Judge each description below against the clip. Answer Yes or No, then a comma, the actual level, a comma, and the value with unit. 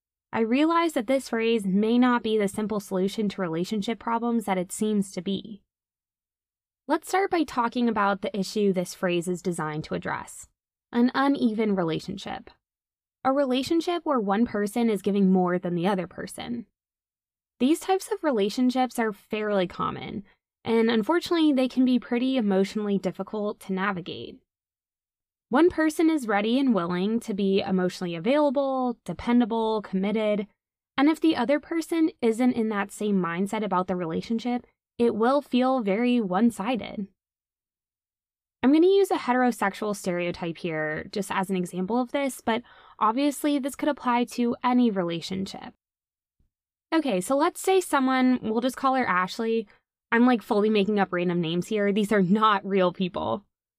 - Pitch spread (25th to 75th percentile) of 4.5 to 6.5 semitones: Yes, average, 4.8 semitones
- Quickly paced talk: No, average, 155 wpm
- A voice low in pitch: No, high, 220 Hz